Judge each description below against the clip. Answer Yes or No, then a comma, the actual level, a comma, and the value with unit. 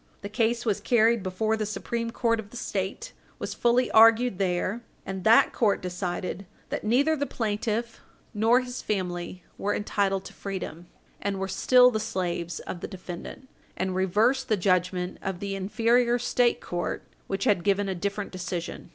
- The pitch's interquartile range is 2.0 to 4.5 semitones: Yes, average, 3.8 semitones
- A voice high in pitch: Yes, high, 205 Hz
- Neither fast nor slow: Yes, average, 170 wpm